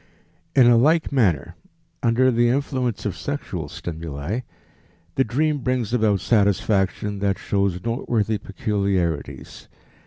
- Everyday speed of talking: No, slow, 115 wpm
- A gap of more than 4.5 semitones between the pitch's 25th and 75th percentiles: No, average, 4.1 semitones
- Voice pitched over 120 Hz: No, low, 110 Hz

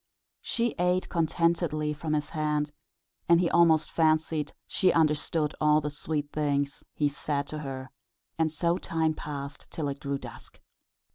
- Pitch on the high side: No, medium, 155 Hz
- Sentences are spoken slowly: No, average, 150 wpm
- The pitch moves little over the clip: Yes, narrow, 1.9 semitones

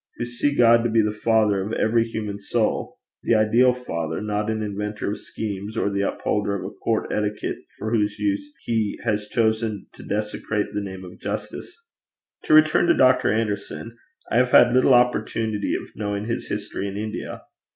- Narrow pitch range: Yes, narrow, 2.3 semitones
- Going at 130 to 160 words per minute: No, average, 180 wpm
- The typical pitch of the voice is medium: No, low, 110 Hz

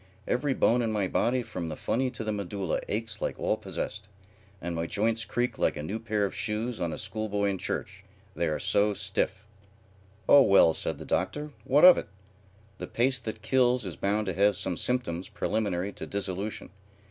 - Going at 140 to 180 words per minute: No, average, 195 wpm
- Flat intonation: No, average, 3.4 semitones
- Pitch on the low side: Yes, low, 105 Hz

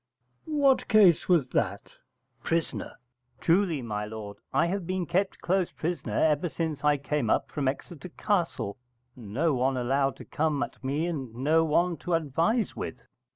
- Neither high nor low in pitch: Yes, medium, 155 Hz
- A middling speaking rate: Yes, average, 165 wpm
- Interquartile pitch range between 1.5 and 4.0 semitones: No, average, 4.6 semitones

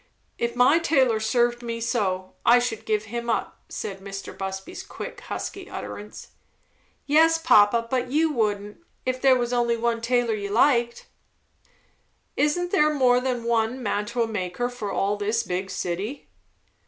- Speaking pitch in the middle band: No, high, 235 Hz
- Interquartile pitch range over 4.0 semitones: No, average, 3.4 semitones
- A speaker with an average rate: Yes, average, 150 wpm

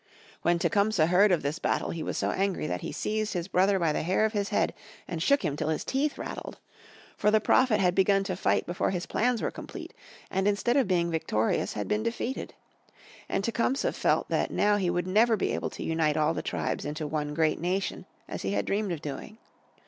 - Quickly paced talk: Yes, fast, 220 wpm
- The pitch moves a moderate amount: Yes, average, 4.5 semitones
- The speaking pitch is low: No, medium, 185 Hz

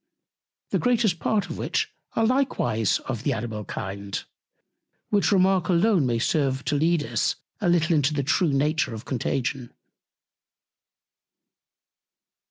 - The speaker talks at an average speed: No, slow, 130 wpm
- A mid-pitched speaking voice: Yes, medium, 150 Hz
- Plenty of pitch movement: Yes, wide, 7.3 semitones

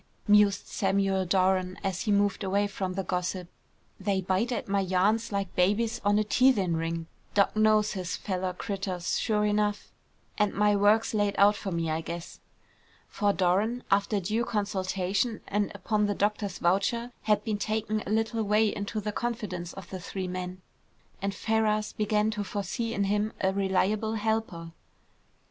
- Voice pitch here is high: Yes, high, 200 Hz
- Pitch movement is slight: Yes, narrow, 2.2 semitones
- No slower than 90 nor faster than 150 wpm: No, average, 165 wpm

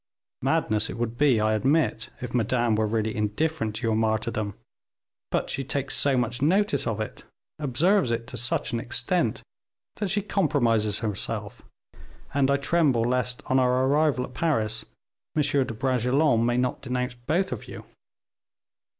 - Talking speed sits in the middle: Yes, average, 160 wpm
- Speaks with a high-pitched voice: No, low, 125 Hz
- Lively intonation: No, average, 4.0 semitones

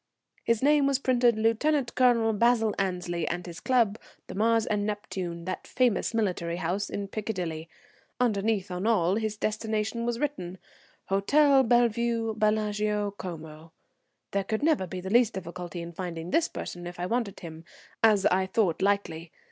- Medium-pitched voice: No, high, 210 Hz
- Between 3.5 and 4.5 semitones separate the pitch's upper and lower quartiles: Yes, average, 4.2 semitones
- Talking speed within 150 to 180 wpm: Yes, average, 155 wpm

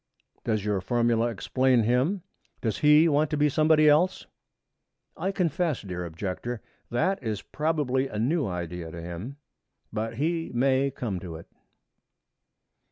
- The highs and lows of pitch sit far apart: Yes, wide, 6.5 semitones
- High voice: No, low, 125 Hz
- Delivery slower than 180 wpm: Yes, average, 145 wpm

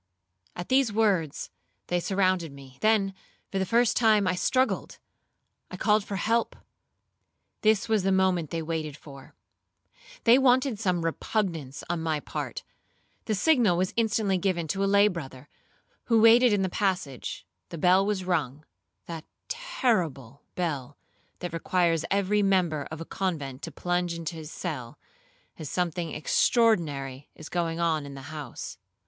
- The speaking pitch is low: No, medium, 180 Hz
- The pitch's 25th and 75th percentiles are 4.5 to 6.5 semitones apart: Yes, average, 4.8 semitones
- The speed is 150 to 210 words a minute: No, average, 140 wpm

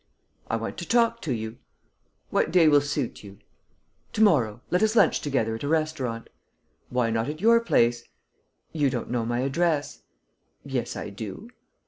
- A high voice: No, medium, 140 Hz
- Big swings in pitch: Yes, wide, 6.8 semitones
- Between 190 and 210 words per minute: No, average, 165 wpm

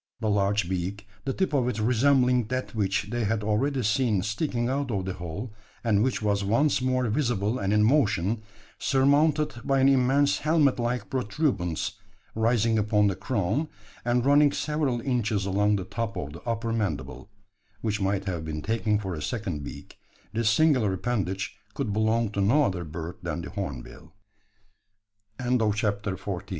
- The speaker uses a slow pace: No, average, 165 wpm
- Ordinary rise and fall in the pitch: Yes, average, 4.3 semitones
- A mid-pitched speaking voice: No, low, 110 Hz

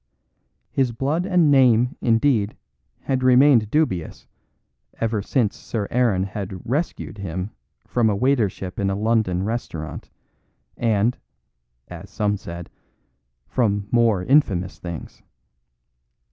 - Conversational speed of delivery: No, slow, 110 wpm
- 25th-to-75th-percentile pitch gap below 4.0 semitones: No, average, 4.5 semitones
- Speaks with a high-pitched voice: No, low, 110 Hz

